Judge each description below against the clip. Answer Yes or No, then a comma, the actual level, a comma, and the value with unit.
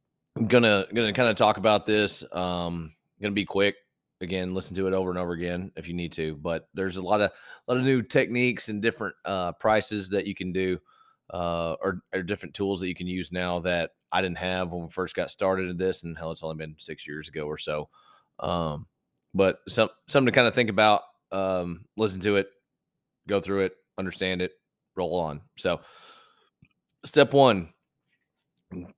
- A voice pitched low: Yes, very low, 95 Hz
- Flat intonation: No, average, 3.1 semitones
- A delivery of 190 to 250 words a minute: Yes, average, 195 wpm